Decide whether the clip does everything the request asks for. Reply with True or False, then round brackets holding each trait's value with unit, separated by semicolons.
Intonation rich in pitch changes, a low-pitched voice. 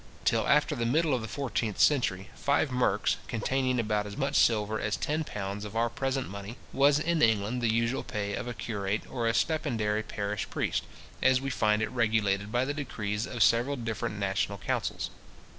False (4.1 semitones; 115 Hz)